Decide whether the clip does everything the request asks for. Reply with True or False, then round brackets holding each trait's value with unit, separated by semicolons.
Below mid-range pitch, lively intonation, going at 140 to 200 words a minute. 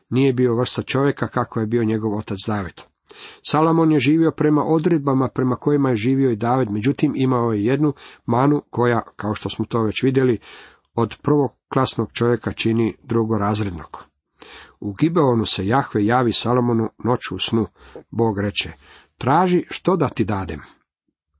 False (120 Hz; 4.1 semitones; 155 wpm)